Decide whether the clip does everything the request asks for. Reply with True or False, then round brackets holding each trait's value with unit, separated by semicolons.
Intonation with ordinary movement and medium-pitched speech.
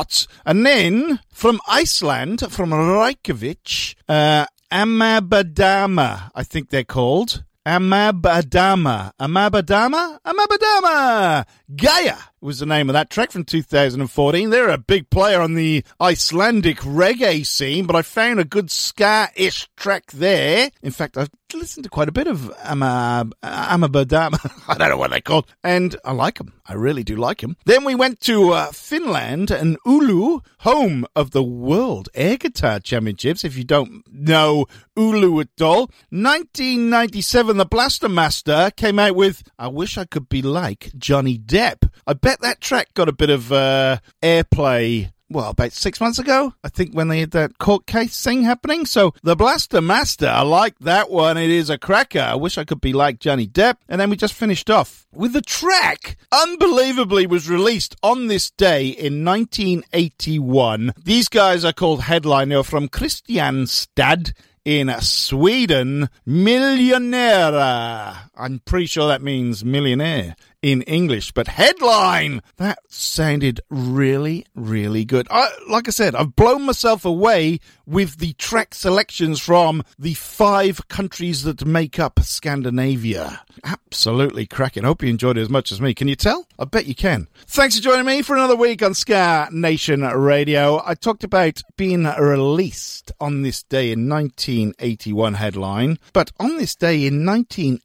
False (7.1 semitones; 165 Hz)